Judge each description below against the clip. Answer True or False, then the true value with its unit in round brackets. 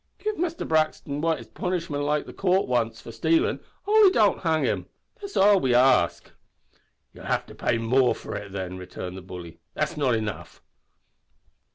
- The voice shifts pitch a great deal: True (8.2 semitones)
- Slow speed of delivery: False (165 wpm)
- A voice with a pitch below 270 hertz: True (140 Hz)